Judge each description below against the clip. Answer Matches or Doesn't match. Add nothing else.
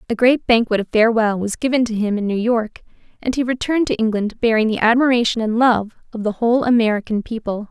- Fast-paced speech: Matches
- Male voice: Doesn't match